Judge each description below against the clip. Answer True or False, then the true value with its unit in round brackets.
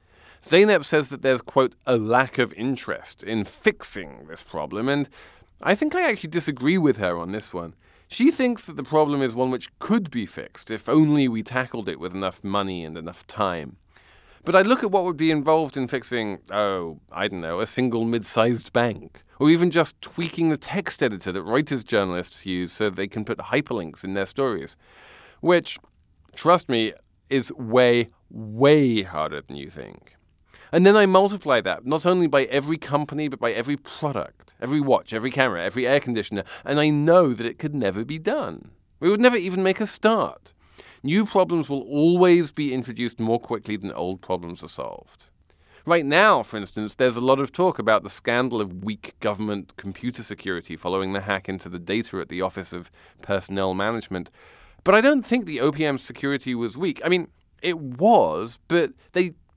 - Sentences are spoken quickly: False (190 wpm)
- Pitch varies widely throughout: True (7.5 semitones)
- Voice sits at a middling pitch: False (125 Hz)